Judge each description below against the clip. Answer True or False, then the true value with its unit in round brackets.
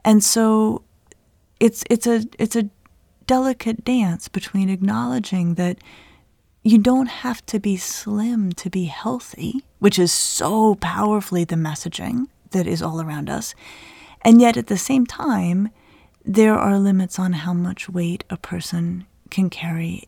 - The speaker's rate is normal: True (145 wpm)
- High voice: True (205 Hz)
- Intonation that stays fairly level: False (4.2 semitones)